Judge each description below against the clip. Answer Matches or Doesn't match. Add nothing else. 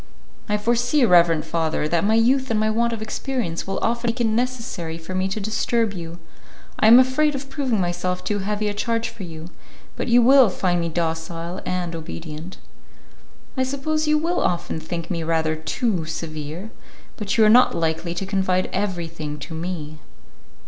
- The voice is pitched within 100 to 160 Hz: Doesn't match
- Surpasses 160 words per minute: Matches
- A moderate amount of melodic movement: Doesn't match